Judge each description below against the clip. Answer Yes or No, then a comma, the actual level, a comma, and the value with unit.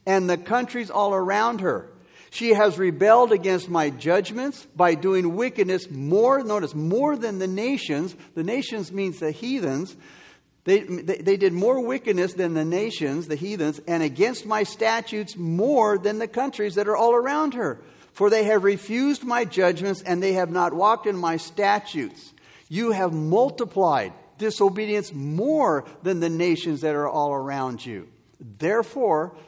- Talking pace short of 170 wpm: Yes, average, 160 wpm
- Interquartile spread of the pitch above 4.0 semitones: Yes, average, 4.8 semitones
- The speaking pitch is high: Yes, high, 195 Hz